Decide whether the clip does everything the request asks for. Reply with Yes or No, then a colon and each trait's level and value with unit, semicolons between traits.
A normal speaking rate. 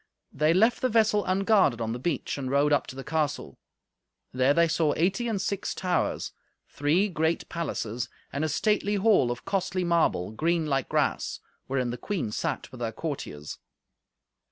Yes: average, 170 wpm